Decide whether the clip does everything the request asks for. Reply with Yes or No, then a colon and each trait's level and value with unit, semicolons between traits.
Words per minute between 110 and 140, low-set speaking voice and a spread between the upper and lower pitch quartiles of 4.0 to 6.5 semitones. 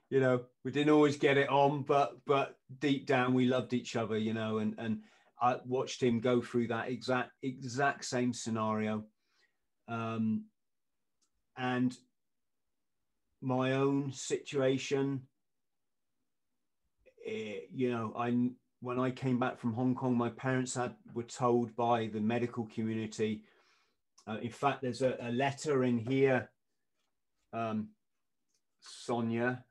No: slow, 135 wpm; low, 125 Hz; narrow, 2.4 semitones